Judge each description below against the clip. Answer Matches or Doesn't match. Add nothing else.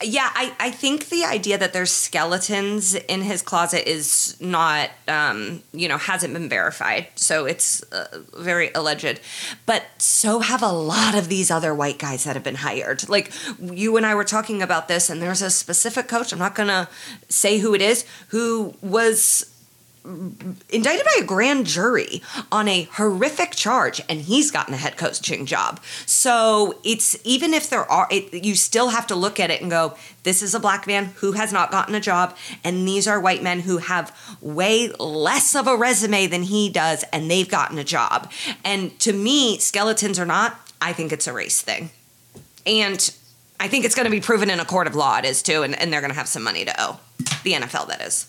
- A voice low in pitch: Doesn't match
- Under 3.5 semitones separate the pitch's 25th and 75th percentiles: Doesn't match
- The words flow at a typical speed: Doesn't match